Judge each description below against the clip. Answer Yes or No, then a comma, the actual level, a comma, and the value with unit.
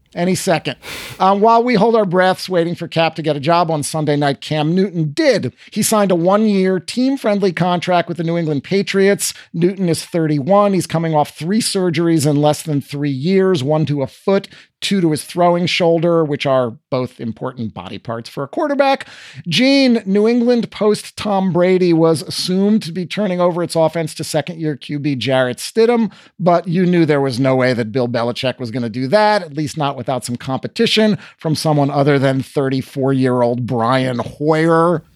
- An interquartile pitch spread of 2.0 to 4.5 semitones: No, average, 5.2 semitones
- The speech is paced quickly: No, average, 195 wpm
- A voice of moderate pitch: Yes, medium, 165 Hz